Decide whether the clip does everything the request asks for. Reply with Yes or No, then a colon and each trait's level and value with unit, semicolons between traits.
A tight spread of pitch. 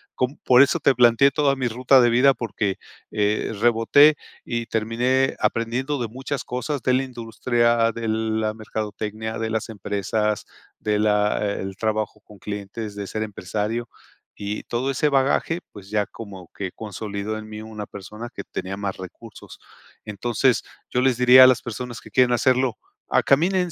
No: average, 3.2 semitones